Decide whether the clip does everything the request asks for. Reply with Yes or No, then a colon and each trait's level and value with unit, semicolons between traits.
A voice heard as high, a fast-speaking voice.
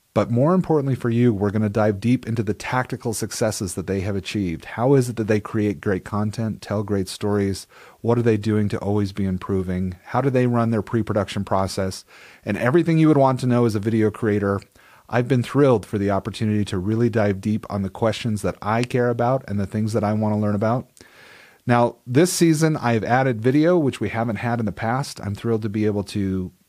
No: low, 110 Hz; fast, 225 wpm